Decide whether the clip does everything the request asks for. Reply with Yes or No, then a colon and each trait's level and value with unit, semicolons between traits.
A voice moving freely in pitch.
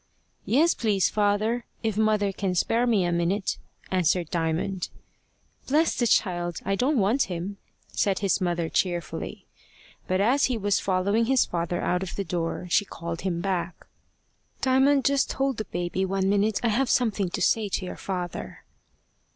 No: average, 4.1 semitones